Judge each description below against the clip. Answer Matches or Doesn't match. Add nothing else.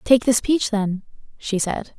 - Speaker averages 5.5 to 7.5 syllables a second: Doesn't match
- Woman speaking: Matches